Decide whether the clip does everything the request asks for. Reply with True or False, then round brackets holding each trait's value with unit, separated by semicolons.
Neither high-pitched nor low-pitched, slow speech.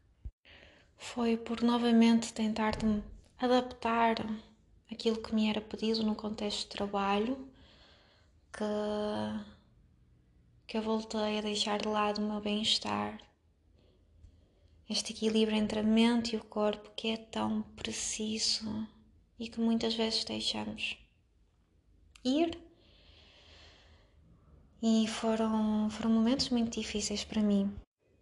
False (215 Hz; 110 wpm)